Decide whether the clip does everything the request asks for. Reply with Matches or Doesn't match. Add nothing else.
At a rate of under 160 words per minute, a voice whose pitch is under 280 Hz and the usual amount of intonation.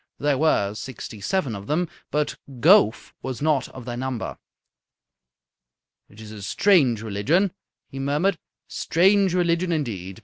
Doesn't match